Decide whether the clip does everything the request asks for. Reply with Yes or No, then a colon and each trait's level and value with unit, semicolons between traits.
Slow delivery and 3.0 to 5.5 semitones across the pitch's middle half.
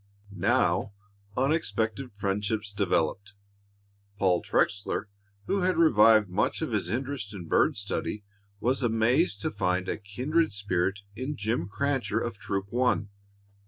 Yes: slow, 125 wpm; average, 4.1 semitones